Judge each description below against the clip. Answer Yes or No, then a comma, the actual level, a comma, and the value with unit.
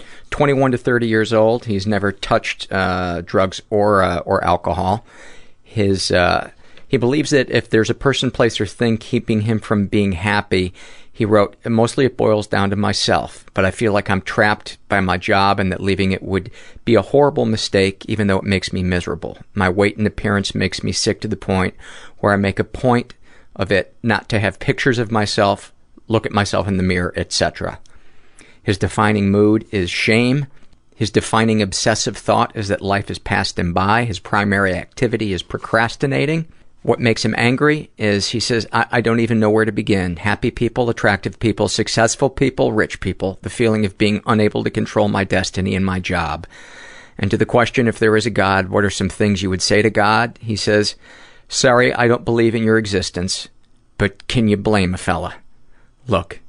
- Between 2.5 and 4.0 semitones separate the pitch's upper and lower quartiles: Yes, average, 3.0 semitones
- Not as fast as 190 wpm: No, average, 195 wpm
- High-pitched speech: No, low, 105 Hz